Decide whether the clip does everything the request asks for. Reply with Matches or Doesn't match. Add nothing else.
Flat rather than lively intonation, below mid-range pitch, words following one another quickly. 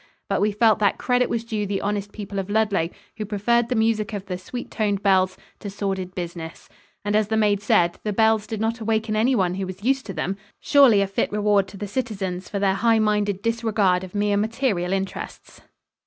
Doesn't match